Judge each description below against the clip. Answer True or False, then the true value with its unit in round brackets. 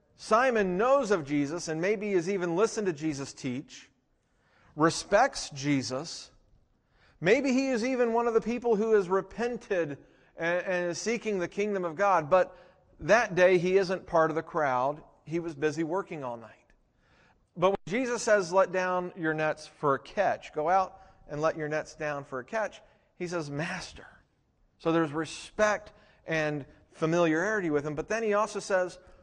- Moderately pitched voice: True (180 Hz)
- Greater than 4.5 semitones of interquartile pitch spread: True (4.9 semitones)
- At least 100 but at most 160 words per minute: False (170 wpm)